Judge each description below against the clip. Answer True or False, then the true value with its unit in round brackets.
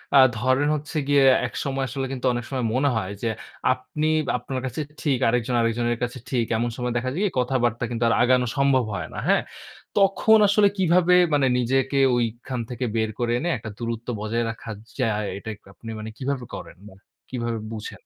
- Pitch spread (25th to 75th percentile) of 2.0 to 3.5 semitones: True (2.8 semitones)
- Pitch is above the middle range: False (125 Hz)